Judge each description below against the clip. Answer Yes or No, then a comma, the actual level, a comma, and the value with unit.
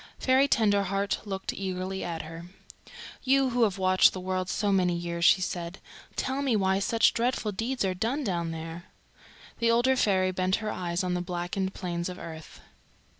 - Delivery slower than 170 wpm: No, average, 175 wpm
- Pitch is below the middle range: No, high, 190 Hz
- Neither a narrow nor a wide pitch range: Yes, average, 3.9 semitones